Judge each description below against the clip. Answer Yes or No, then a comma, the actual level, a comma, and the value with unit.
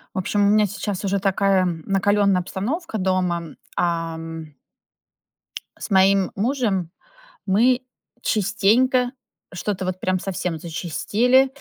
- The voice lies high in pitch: Yes, high, 195 Hz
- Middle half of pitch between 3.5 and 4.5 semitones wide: No, average, 2.9 semitones